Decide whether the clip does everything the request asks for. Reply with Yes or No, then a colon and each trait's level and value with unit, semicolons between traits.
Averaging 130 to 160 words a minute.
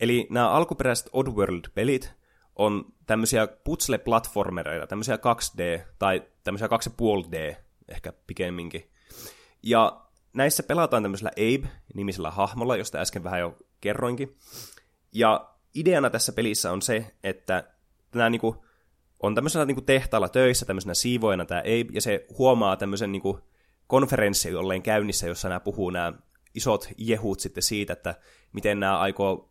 No: average, 120 wpm